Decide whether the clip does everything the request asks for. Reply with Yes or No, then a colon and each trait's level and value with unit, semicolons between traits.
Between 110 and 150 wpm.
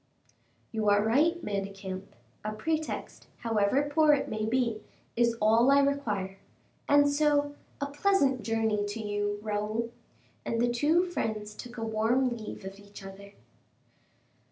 Yes: average, 140 wpm